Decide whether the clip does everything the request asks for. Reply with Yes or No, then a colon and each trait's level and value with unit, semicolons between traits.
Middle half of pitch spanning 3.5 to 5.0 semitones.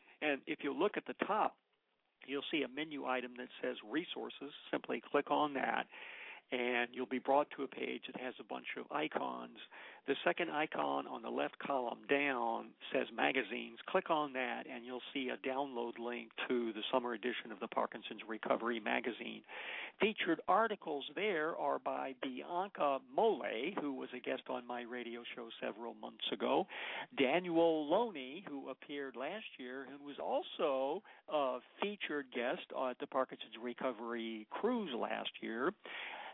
No: average, 2.9 semitones